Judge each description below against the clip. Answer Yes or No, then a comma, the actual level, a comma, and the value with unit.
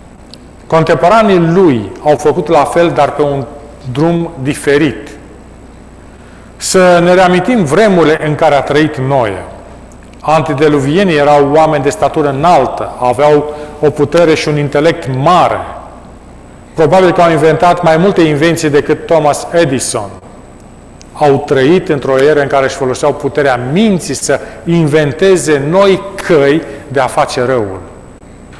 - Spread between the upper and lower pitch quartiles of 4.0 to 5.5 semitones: No, average, 3.2 semitones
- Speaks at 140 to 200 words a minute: No, average, 130 wpm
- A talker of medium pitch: Yes, medium, 150 Hz